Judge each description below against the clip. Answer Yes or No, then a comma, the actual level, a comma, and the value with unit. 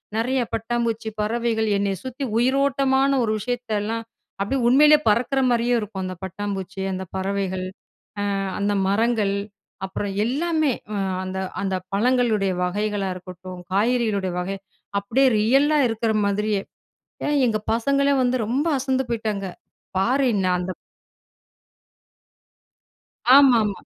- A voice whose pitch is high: Yes, high, 220 Hz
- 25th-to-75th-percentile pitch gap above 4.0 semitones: Yes, average, 4.4 semitones